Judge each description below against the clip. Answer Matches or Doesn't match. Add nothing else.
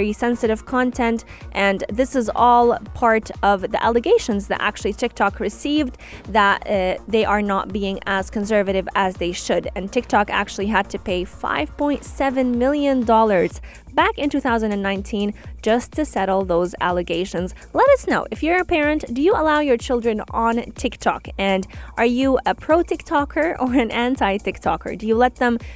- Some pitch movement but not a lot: Matches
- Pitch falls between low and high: Doesn't match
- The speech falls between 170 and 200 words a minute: Doesn't match